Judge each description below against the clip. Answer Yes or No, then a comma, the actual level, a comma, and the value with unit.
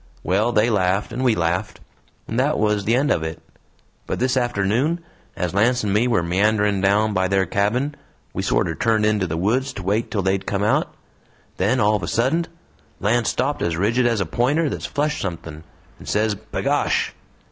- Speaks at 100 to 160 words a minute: No, average, 190 wpm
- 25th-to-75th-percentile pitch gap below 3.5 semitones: No, average, 4.0 semitones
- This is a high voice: No, low, 105 Hz